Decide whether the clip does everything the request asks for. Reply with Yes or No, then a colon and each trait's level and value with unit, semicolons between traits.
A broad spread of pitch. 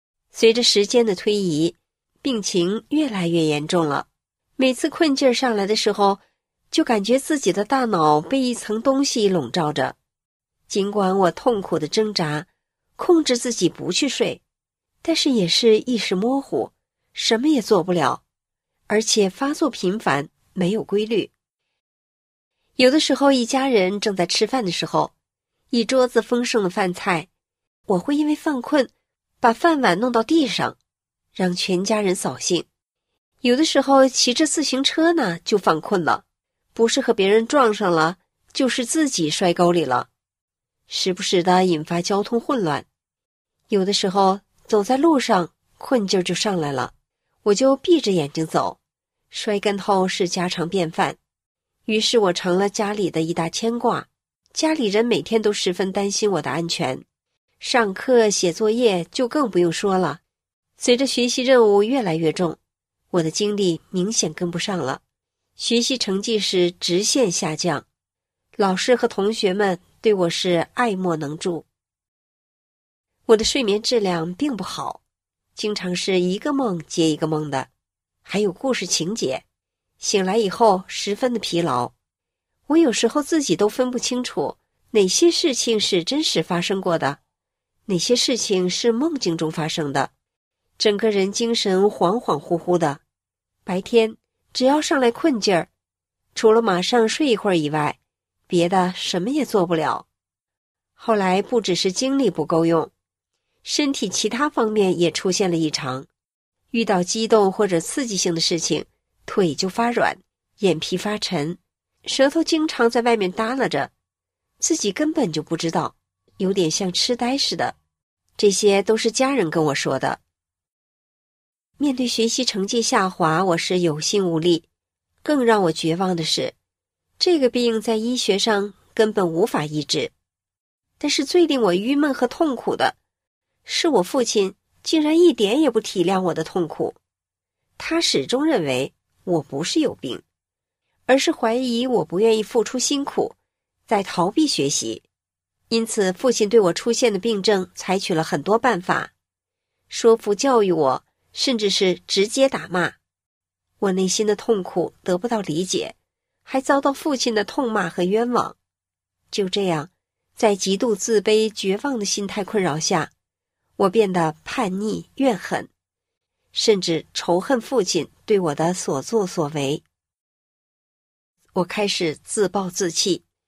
Yes: wide, 5.8 semitones